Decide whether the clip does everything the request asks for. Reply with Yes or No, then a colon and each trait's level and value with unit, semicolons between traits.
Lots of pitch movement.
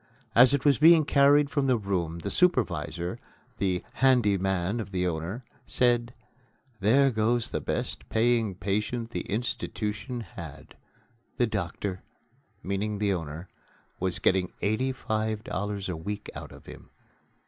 No: average, 4.2 semitones